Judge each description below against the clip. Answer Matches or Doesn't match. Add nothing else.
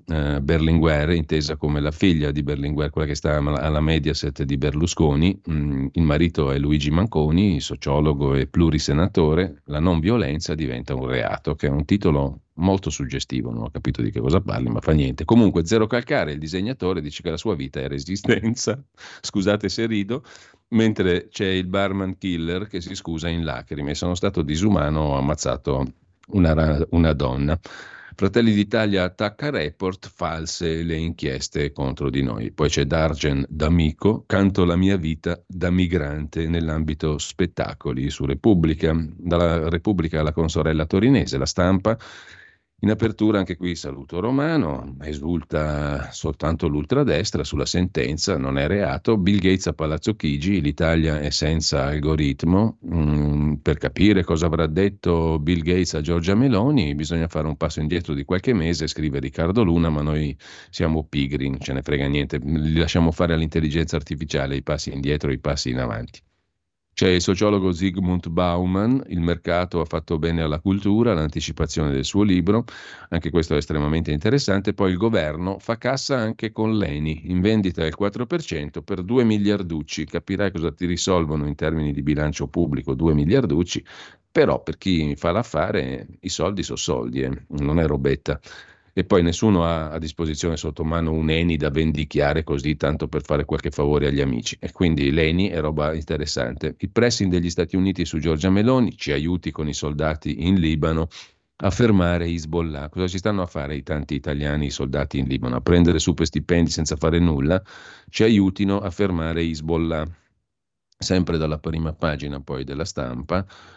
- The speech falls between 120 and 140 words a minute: Doesn't match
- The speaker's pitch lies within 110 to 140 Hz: Doesn't match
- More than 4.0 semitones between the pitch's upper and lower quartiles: Doesn't match